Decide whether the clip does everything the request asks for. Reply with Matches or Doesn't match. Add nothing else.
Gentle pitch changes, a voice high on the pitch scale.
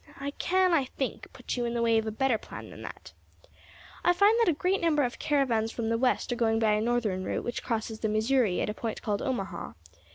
Doesn't match